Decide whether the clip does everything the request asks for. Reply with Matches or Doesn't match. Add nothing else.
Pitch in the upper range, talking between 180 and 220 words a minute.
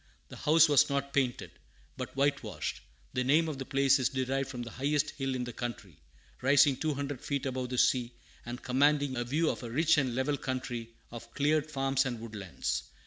Doesn't match